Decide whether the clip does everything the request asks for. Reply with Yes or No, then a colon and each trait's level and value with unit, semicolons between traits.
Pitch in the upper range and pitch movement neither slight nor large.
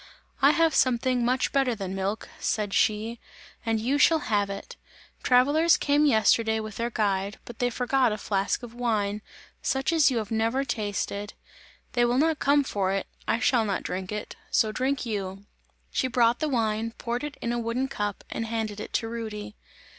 Yes: high, 230 Hz; average, 3.3 semitones